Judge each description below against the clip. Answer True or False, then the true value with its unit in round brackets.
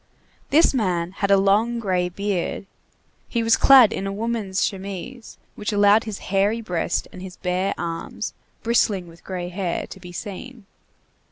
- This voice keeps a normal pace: True (160 wpm)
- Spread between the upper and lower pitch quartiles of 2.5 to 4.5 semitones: True (3.6 semitones)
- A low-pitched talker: False (195 Hz)